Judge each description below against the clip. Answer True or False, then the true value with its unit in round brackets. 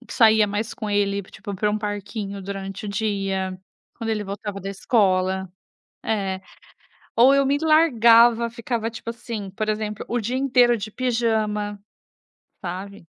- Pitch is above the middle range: True (210 Hz)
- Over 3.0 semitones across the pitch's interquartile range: False (2.7 semitones)